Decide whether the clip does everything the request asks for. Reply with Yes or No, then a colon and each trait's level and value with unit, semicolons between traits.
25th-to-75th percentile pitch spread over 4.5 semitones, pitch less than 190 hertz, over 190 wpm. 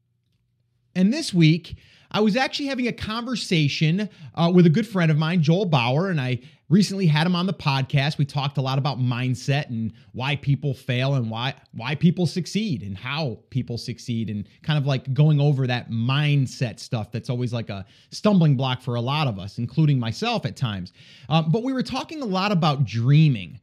Yes: wide, 5.6 semitones; medium, 140 Hz; average, 200 wpm